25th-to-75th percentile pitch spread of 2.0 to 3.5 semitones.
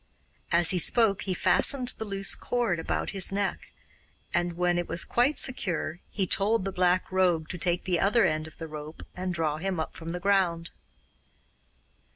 Yes: average, 2.7 semitones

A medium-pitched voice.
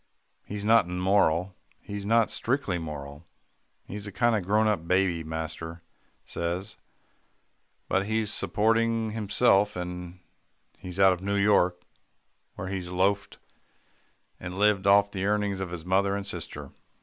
No: very low, 95 Hz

